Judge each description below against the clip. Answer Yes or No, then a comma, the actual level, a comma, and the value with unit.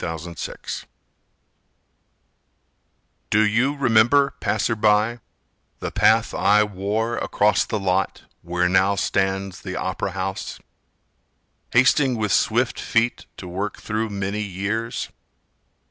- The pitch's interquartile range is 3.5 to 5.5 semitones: No, average, 2.8 semitones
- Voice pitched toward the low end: Yes, low, 105 Hz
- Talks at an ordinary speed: No, slow, 110 wpm